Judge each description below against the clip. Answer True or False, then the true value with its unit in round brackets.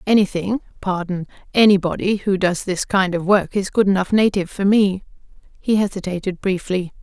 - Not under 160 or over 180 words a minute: False (135 wpm)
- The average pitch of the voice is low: False (190 Hz)